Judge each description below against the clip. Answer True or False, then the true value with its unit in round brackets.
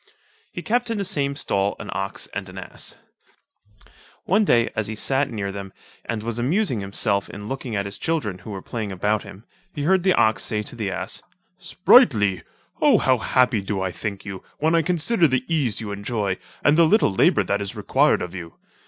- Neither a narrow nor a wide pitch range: False (6.4 semitones)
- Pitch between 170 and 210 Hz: False (110 Hz)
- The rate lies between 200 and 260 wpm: True (205 wpm)